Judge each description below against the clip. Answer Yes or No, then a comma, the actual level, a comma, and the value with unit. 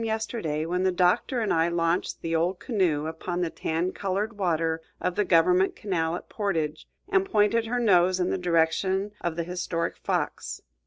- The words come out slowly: No, average, 175 wpm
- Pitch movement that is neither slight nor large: Yes, average, 3.5 semitones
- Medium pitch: Yes, medium, 180 Hz